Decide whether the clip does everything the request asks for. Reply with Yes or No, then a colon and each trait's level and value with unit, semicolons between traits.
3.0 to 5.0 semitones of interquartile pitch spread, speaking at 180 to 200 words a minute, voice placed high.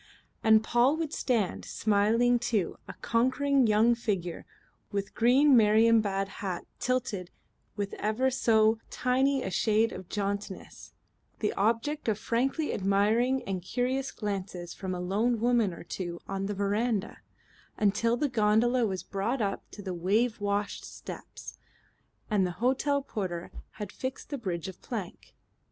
No: average, 3.8 semitones; average, 140 wpm; high, 215 Hz